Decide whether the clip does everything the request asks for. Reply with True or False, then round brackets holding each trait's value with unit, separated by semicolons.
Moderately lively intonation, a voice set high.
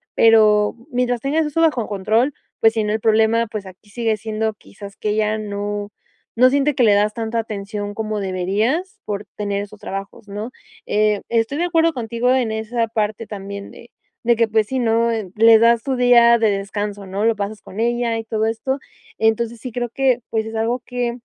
False (2.3 semitones; 220 Hz)